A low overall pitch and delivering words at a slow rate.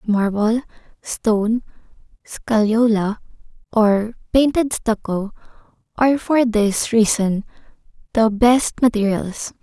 No: high, 225 Hz; slow, 80 wpm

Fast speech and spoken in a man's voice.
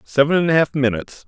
Yes: fast, 235 wpm; male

